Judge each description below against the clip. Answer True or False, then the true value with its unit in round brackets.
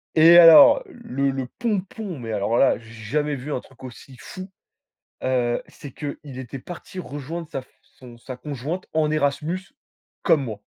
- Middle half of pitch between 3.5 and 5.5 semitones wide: True (4.6 semitones)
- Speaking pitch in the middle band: True (145 Hz)